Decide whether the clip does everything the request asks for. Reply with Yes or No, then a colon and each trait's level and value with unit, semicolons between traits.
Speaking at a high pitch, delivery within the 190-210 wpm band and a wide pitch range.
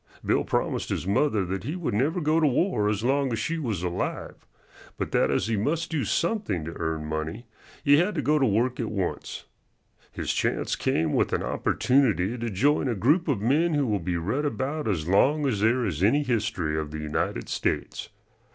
No: low, 115 Hz; fast, 205 wpm; wide, 7.4 semitones